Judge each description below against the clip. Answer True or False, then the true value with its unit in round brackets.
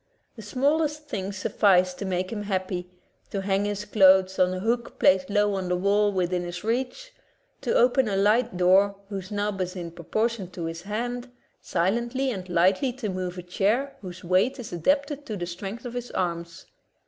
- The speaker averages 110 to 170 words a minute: False (195 wpm)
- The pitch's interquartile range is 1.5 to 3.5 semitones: False (4.3 semitones)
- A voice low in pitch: False (200 Hz)